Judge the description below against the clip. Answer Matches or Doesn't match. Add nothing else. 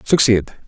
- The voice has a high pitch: Doesn't match